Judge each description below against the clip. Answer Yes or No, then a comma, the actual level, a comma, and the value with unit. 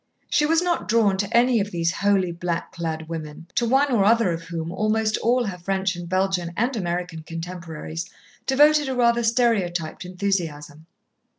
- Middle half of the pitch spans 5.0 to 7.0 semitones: Yes, wide, 5.5 semitones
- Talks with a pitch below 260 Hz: Yes, high, 190 Hz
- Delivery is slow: No, average, 170 wpm